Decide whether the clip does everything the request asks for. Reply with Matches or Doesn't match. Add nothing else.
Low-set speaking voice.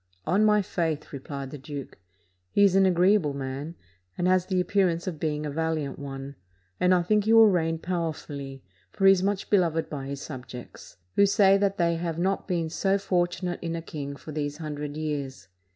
Doesn't match